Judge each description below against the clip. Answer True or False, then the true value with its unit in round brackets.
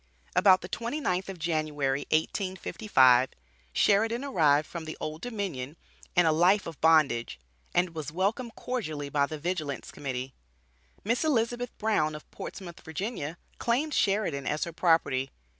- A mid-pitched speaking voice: True (170 Hz)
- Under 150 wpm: True (140 wpm)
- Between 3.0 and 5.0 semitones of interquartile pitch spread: False (5.6 semitones)